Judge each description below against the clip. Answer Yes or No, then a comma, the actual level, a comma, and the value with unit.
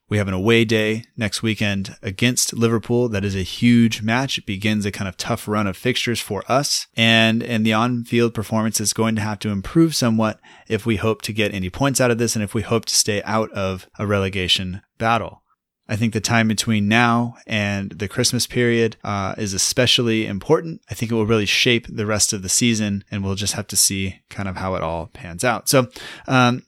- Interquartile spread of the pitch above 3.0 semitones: No, average, 2.7 semitones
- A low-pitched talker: Yes, low, 110 Hz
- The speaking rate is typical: No, fast, 225 wpm